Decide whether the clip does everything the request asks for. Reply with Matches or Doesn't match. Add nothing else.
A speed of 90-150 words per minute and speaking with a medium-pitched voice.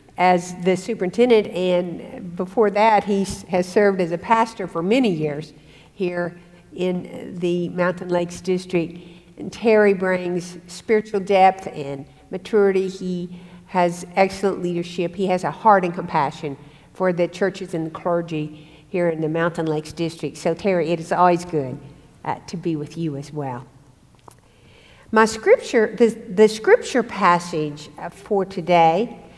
Matches